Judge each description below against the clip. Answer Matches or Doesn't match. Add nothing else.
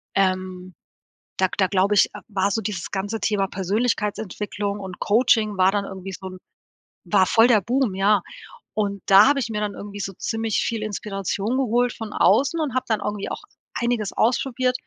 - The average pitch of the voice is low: Doesn't match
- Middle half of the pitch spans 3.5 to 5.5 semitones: Doesn't match